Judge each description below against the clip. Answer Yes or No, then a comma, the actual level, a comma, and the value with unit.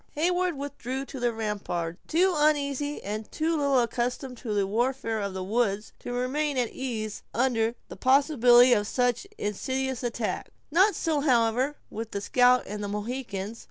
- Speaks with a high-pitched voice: Yes, high, 245 Hz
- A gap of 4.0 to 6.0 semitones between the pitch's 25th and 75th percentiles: Yes, average, 4.4 semitones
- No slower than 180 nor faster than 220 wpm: No, average, 160 wpm